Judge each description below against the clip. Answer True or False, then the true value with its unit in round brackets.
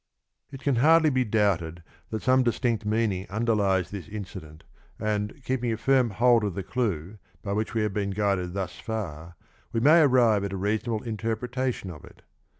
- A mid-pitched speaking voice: False (110 Hz)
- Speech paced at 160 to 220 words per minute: True (180 wpm)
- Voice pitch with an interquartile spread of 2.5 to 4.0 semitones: True (3.6 semitones)